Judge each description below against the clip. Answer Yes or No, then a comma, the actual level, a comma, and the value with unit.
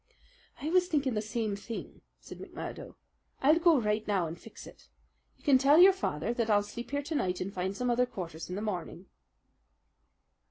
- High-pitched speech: Yes, high, 225 Hz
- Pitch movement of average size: No, wide, 6.2 semitones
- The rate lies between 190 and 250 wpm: Yes, average, 195 wpm